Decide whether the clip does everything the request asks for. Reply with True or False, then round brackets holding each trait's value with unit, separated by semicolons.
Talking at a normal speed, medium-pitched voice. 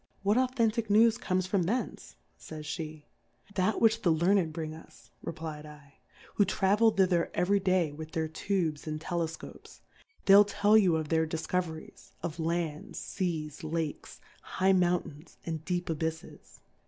True (155 wpm; 170 Hz)